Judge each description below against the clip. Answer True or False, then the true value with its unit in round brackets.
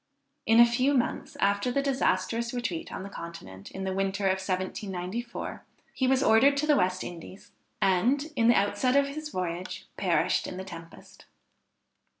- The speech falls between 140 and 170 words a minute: True (160 wpm)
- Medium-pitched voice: False (205 Hz)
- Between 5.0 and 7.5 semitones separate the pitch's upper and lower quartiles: True (5.4 semitones)